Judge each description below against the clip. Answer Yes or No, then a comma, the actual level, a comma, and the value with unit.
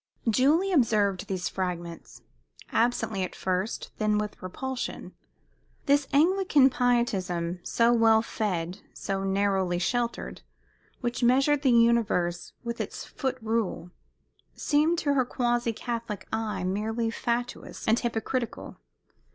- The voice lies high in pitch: Yes, high, 230 Hz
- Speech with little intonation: No, average, 4.3 semitones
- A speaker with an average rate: No, slow, 115 wpm